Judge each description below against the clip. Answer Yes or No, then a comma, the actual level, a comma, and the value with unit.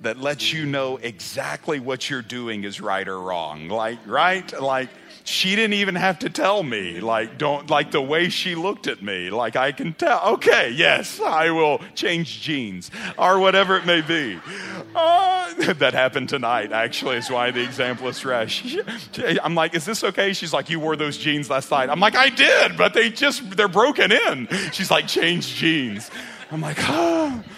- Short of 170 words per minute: No, average, 185 wpm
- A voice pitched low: No, medium, 160 Hz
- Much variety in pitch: Yes, wide, 7.5 semitones